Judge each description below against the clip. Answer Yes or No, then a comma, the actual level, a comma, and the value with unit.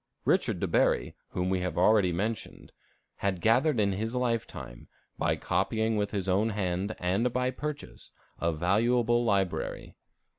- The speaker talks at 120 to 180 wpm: Yes, average, 150 wpm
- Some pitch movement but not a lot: Yes, average, 4.1 semitones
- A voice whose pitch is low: Yes, low, 105 Hz